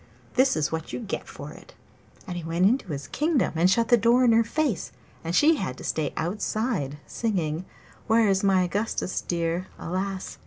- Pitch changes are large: Yes, wide, 5.7 semitones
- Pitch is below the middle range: No, high, 190 Hz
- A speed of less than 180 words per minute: No, average, 185 wpm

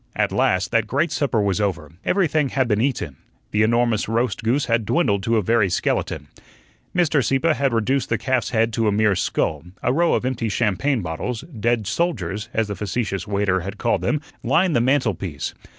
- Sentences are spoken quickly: No, average, 190 wpm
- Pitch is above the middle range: No, low, 115 Hz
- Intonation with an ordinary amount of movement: Yes, average, 4.5 semitones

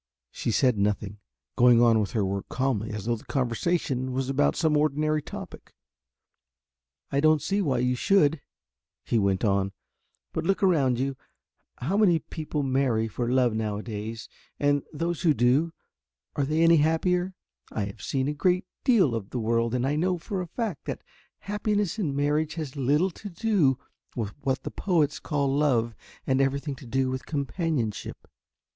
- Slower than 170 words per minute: No, average, 175 wpm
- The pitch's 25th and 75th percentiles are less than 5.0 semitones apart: No, wide, 5.4 semitones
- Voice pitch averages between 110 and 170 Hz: Yes, low, 135 Hz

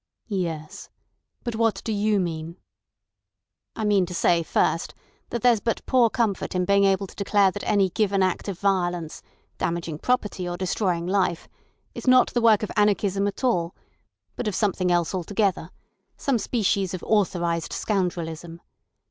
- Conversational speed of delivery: Yes, average, 150 wpm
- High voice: Yes, high, 195 Hz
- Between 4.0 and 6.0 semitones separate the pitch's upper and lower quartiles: No, average, 3.3 semitones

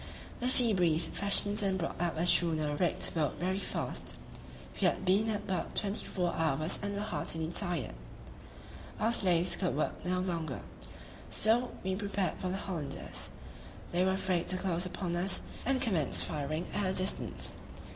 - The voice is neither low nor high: Yes, medium, 180 Hz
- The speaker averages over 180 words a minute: No, average, 165 wpm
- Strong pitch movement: No, average, 3.2 semitones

